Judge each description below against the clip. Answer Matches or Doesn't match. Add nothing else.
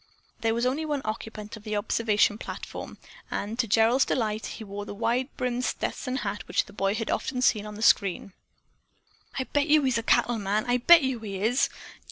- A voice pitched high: Matches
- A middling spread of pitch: Matches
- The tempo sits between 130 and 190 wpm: Doesn't match